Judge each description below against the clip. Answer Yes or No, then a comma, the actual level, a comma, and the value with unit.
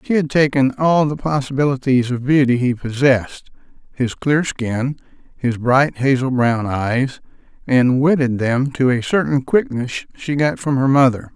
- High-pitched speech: No, low, 135 Hz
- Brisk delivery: No, average, 160 wpm